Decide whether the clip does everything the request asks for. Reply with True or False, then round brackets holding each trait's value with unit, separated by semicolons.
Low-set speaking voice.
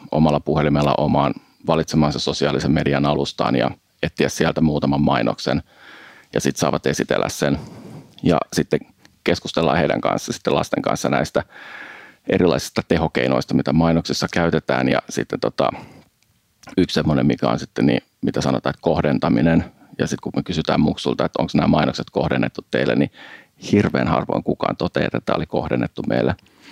True (70 Hz)